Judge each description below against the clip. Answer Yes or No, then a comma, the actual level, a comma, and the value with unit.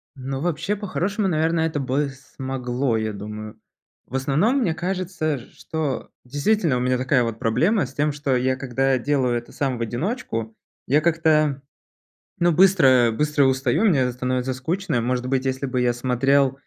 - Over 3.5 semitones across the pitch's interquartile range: Yes, average, 4.1 semitones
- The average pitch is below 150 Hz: Yes, low, 135 Hz